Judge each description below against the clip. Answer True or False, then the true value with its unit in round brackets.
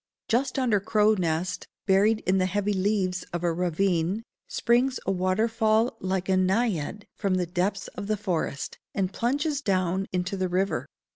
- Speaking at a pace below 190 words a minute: True (160 wpm)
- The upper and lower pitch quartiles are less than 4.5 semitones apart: True (2.9 semitones)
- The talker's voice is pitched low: False (195 Hz)